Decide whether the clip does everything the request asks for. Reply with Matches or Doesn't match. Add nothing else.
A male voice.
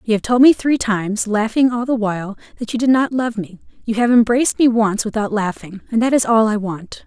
Doesn't match